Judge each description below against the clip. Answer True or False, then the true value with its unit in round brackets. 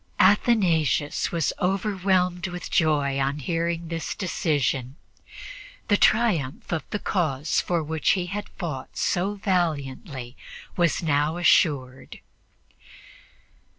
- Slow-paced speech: True (105 wpm)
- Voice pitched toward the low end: False (165 Hz)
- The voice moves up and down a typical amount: True (4.2 semitones)